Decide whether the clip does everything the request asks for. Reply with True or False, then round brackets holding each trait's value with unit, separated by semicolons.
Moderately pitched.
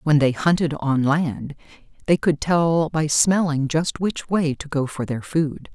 True (150 Hz)